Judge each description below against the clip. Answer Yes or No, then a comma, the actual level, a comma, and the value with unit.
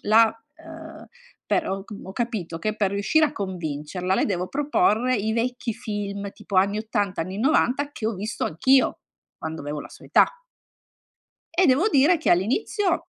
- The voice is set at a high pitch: Yes, high, 215 Hz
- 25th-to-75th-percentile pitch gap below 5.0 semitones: No, wide, 5.9 semitones